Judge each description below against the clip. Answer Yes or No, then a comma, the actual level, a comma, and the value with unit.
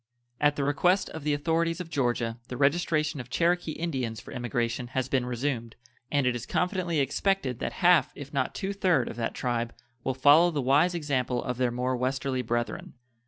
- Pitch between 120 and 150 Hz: Yes, low, 135 Hz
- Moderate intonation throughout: Yes, average, 4.8 semitones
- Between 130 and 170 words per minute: No, average, 190 wpm